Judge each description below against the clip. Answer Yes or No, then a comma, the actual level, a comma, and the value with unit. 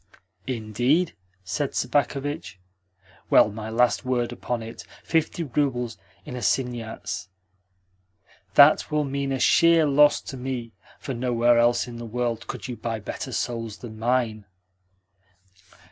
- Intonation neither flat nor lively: Yes, average, 3.1 semitones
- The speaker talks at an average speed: No, slow, 130 wpm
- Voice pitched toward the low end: Yes, low, 125 Hz